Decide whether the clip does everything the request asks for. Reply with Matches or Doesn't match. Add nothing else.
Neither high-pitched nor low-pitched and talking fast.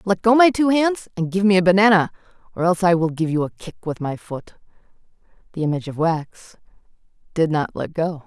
Matches